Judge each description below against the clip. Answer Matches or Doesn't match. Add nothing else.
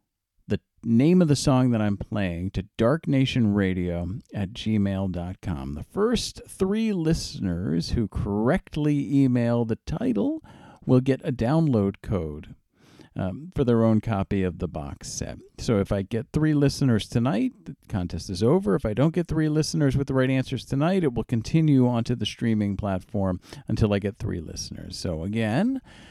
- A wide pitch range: Matches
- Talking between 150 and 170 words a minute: Matches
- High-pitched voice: Doesn't match